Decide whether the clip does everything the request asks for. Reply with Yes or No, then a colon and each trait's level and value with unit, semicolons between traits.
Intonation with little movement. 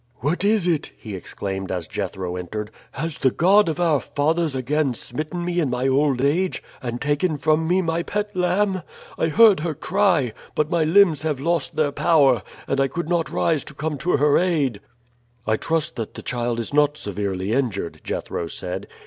No: wide, 5.6 semitones